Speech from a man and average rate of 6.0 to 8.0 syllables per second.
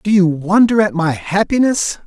No: male; 4.6 syllables/s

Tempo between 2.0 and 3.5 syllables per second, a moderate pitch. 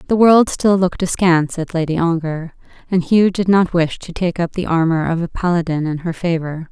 No: 5.3 syllables/s; medium, 170 Hz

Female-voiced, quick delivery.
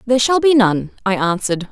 Yes: female; fast, 210 wpm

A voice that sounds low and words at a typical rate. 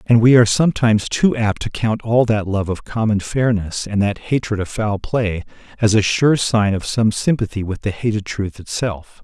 No: low, 110 Hz; fast, 210 wpm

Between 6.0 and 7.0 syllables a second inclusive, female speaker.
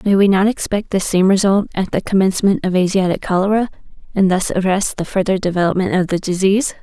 Yes: 6.2 syllables/s; female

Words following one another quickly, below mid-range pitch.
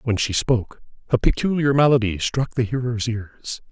No: average, 160 wpm; low, 120 Hz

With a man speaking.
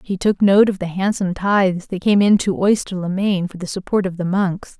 No: female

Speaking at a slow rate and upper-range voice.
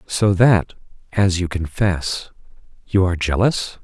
No: slow, 125 wpm; very low, 95 Hz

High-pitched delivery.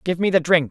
No: medium, 170 Hz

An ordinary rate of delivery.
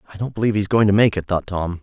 No: fast, 330 wpm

